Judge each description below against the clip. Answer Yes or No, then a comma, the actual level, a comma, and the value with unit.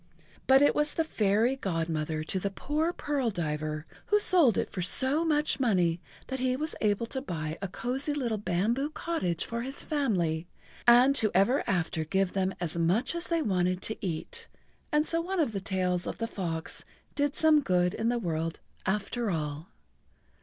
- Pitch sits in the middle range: No, high, 215 Hz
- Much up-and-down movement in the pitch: Yes, wide, 8.0 semitones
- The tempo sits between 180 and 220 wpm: Yes, average, 185 wpm